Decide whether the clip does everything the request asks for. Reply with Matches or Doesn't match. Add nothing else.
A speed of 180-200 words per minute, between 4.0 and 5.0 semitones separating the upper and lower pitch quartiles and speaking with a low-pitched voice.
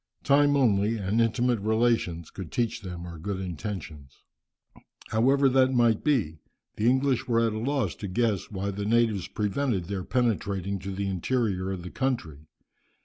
Doesn't match